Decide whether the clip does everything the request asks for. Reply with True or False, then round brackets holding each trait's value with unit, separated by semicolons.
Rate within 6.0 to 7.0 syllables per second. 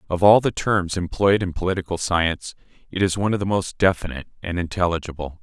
True (6.3 syllables/s)